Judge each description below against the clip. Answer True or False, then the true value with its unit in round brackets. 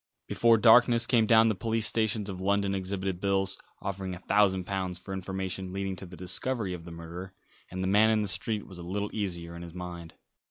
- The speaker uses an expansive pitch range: False (2.5 semitones)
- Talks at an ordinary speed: False (210 wpm)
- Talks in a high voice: False (95 Hz)